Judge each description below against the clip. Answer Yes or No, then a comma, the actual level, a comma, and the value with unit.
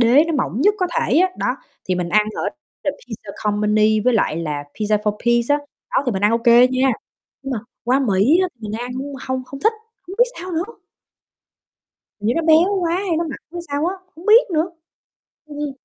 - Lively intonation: Yes, wide, 7.5 semitones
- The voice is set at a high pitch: Yes, very high, 255 Hz